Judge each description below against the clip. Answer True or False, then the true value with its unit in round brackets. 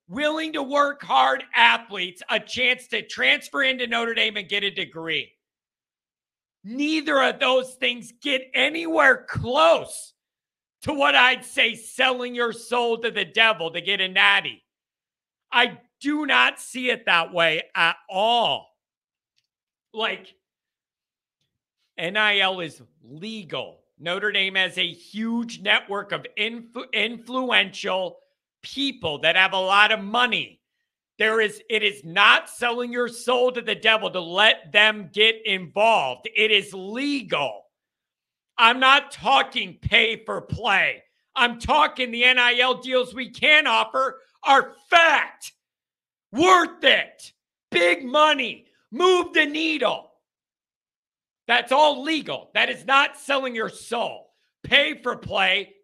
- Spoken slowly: True (130 wpm)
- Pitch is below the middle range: False (235 Hz)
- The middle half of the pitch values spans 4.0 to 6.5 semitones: True (4.5 semitones)